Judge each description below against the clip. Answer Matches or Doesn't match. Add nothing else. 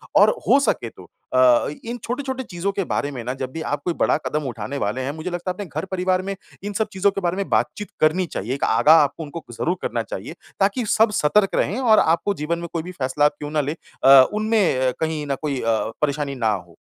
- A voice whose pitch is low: Doesn't match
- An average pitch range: Doesn't match